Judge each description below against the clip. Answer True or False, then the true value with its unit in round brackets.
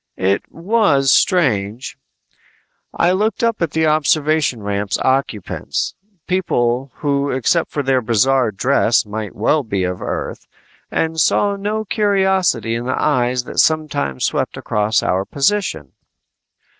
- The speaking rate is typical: False (130 wpm)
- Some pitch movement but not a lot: False (7.0 semitones)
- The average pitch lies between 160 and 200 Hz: False (135 Hz)